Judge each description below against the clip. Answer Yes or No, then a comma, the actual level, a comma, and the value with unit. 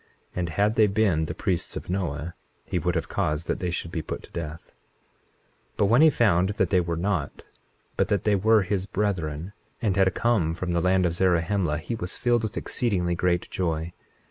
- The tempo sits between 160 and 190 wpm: No, fast, 205 wpm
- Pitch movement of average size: Yes, average, 3.4 semitones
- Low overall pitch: Yes, very low, 90 Hz